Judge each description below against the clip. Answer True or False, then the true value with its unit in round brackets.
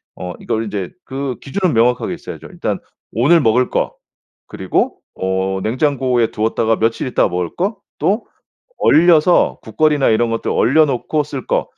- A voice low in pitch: True (125 Hz)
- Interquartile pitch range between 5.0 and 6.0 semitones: True (5.3 semitones)